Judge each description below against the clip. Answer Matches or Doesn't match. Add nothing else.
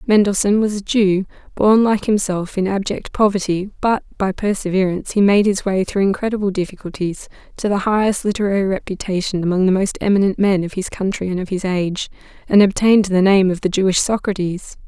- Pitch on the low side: Doesn't match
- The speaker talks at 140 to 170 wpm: Doesn't match